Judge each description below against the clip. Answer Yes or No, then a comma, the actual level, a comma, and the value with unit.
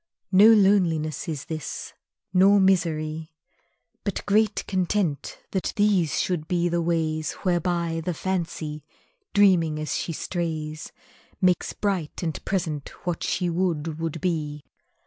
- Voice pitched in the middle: Yes, medium, 170 Hz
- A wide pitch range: No, average, 3.2 semitones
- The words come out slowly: Yes, slow, 125 wpm